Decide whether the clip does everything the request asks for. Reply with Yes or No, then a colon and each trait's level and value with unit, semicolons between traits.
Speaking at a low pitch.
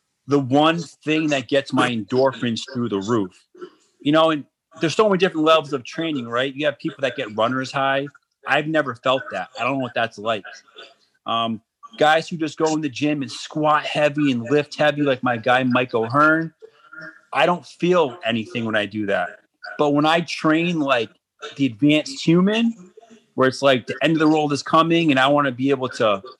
No: medium, 145 Hz